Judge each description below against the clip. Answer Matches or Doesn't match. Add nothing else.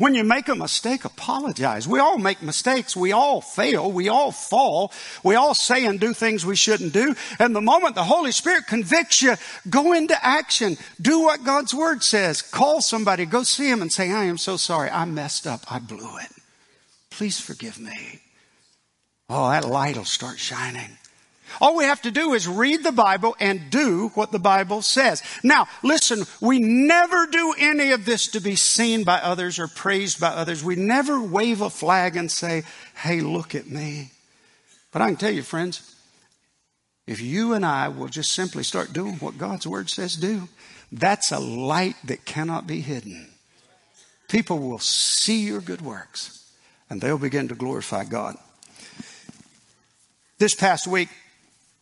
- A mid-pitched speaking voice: Doesn't match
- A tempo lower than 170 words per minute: Doesn't match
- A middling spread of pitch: Doesn't match